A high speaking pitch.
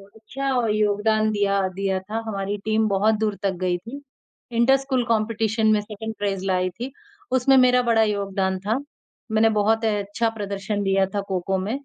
Yes: high, 210 Hz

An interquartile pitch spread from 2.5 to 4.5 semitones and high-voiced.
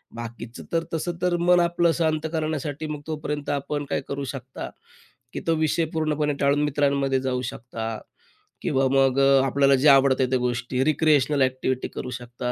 No: average, 3.0 semitones; medium, 140 Hz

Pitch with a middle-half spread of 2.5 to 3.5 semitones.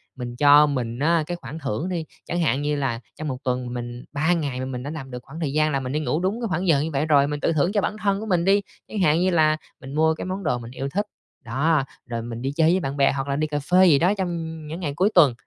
No: average, 4.2 semitones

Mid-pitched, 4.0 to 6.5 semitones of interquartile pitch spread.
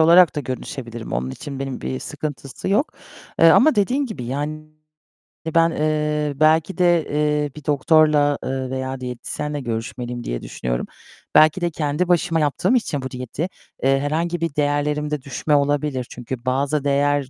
No: medium, 145 Hz; average, 3.0 semitones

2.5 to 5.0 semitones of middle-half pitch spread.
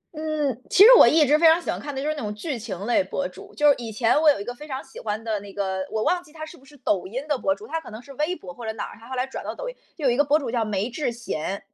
No: wide, 5.5 semitones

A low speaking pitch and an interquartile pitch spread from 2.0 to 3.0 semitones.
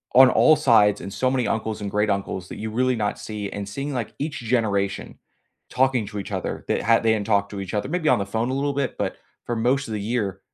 No: low, 110 Hz; average, 4.0 semitones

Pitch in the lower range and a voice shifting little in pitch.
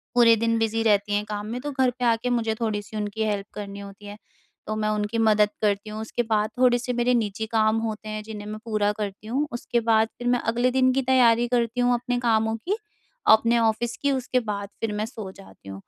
No: high, 220 Hz; narrow, 2.3 semitones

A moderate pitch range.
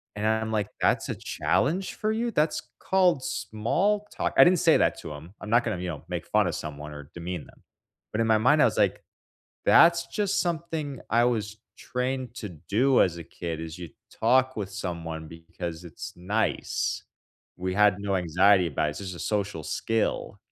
No: wide, 7.1 semitones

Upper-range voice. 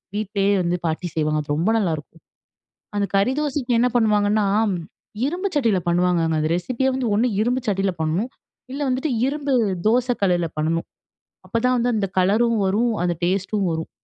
Yes: high, 205 Hz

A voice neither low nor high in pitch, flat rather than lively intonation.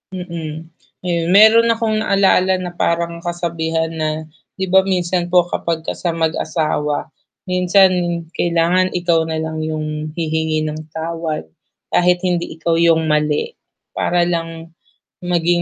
Yes: medium, 170 Hz; narrow, 1.9 semitones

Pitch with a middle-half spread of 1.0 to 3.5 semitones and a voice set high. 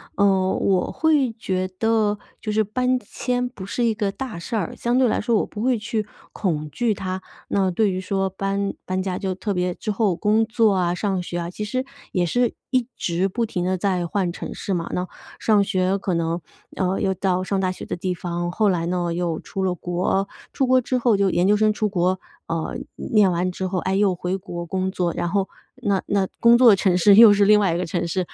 Yes: average, 2.9 semitones; high, 195 Hz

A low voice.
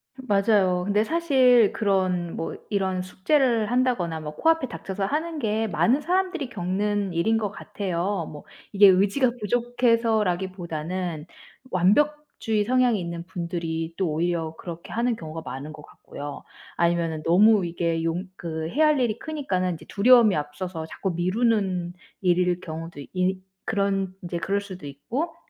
No: high, 190 Hz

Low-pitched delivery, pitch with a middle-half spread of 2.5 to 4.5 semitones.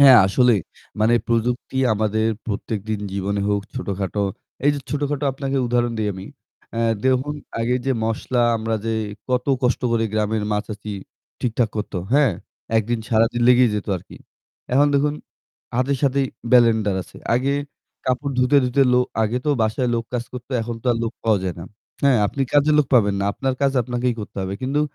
Yes: low, 120 Hz; average, 3.4 semitones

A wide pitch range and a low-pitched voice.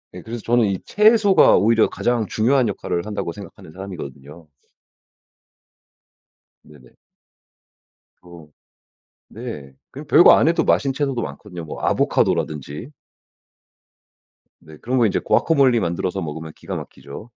Yes: wide, 7.1 semitones; low, 100 Hz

